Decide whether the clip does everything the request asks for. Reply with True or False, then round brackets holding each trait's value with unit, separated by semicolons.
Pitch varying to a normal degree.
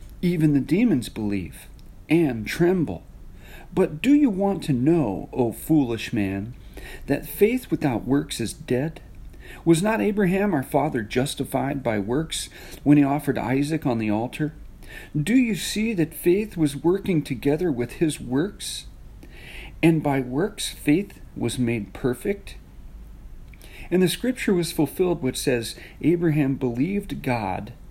False (5.9 semitones)